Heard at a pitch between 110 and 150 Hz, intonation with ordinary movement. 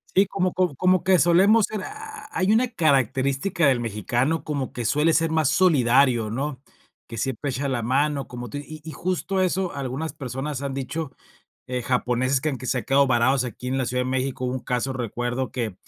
Yes: low, 135 Hz; average, 4.5 semitones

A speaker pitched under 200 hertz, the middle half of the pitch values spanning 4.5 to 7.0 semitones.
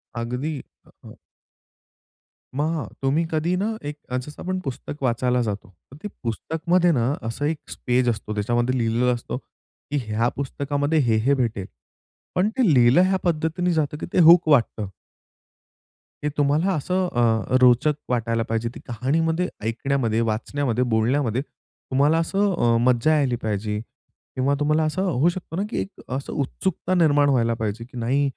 Yes: low, 135 Hz; average, 5.2 semitones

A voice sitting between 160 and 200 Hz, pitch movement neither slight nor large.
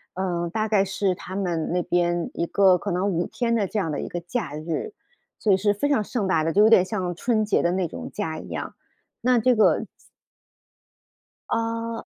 Yes: high, 190 Hz; average, 3.9 semitones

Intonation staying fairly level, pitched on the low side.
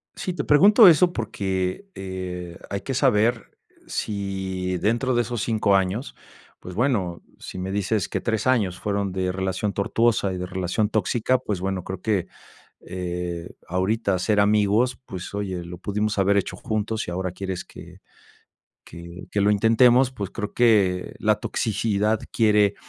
No: average, 3.3 semitones; low, 100 Hz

